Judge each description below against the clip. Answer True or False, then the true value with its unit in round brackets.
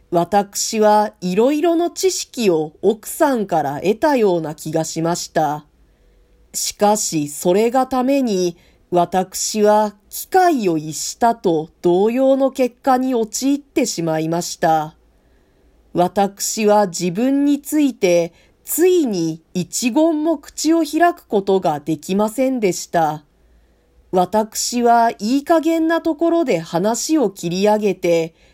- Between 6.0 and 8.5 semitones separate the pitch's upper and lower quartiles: True (7.5 semitones)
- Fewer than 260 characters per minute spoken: True (225 characters per minute)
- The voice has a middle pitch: False (210 Hz)